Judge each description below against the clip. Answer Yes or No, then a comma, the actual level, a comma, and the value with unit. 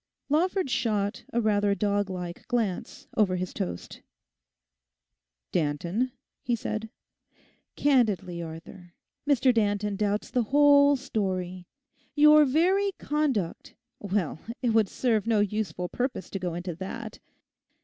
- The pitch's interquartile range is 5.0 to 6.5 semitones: Yes, wide, 5.5 semitones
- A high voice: Yes, high, 210 Hz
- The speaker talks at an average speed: No, slow, 110 wpm